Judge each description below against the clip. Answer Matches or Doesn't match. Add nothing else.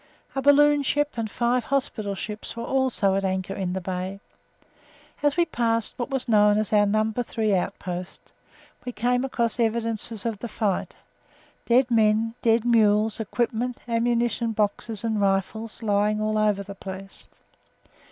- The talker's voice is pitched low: Doesn't match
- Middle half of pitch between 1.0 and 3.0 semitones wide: Matches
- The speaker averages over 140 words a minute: Matches